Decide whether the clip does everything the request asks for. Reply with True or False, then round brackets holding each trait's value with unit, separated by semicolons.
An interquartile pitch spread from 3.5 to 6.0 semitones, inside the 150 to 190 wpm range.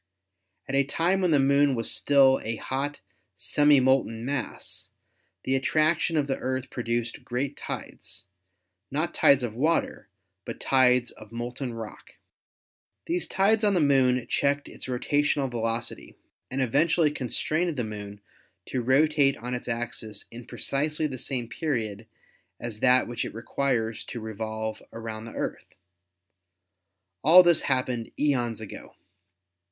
False (3.8 semitones; 140 wpm)